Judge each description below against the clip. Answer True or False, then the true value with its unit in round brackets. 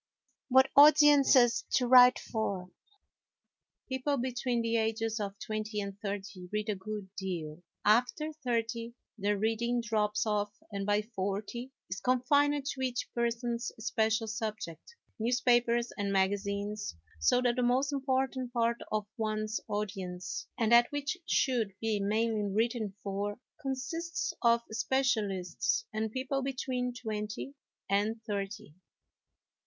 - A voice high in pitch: True (225 Hz)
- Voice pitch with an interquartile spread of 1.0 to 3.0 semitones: False (3.4 semitones)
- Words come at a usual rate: False (125 wpm)